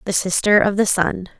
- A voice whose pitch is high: Yes, high, 195 Hz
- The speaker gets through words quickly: Yes, fast, 215 wpm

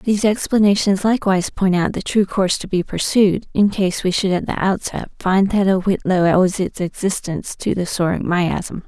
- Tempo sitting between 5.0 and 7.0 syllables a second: Yes, 5.1 syllables/s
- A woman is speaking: Yes, female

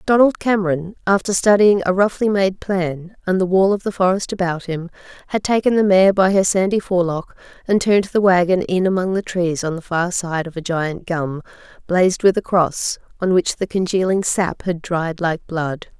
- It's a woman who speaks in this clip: Yes, female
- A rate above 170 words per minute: Yes, average, 200 wpm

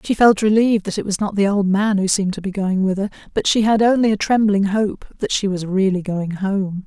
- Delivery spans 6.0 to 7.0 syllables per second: No, 5.5 syllables/s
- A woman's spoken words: Yes, female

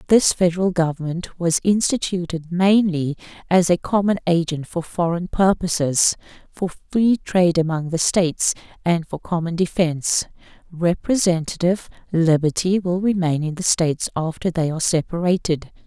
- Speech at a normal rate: No, slow, 130 wpm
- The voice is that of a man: No, female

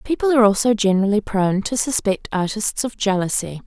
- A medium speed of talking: Yes, average, 165 wpm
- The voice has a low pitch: No, high, 215 Hz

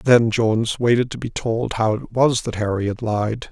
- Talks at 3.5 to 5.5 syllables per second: Yes, 4.6 syllables/s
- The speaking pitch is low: Yes, low, 115 Hz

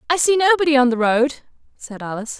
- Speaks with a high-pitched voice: Yes, very high, 275 Hz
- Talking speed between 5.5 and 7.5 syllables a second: Yes, 6.4 syllables/s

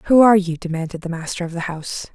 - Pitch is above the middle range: No, medium, 180 Hz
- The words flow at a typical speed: No, fast, 250 wpm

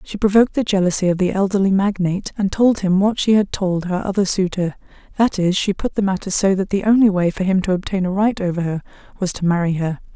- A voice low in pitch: No, high, 190 Hz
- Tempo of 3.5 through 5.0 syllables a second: No, 6.1 syllables/s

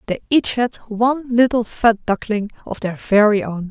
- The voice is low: No, high, 225 Hz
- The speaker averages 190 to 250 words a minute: No, average, 180 wpm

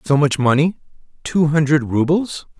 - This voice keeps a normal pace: No, slow, 115 wpm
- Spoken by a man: Yes, male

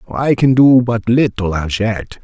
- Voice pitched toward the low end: Yes, low, 110 Hz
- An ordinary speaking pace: Yes, average, 190 wpm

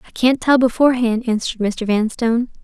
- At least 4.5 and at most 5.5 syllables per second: No, 6.0 syllables/s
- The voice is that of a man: No, female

